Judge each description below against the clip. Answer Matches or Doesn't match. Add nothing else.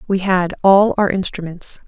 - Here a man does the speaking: Doesn't match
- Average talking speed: Matches